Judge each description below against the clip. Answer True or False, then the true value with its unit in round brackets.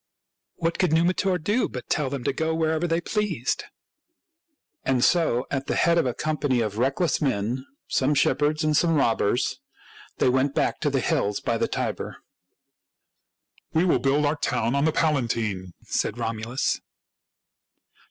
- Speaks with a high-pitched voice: False (145 Hz)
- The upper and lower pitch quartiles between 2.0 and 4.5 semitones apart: False (4.9 semitones)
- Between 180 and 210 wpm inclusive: False (165 wpm)